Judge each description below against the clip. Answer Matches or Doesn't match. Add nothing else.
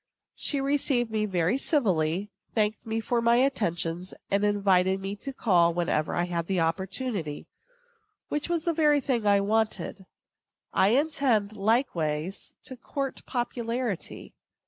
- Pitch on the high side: Matches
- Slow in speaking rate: Matches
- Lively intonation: Matches